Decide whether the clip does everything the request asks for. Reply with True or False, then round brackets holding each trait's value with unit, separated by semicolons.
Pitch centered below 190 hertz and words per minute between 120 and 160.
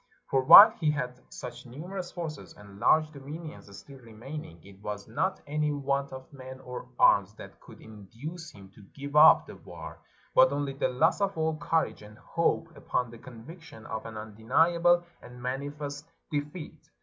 False (140 Hz; 170 wpm)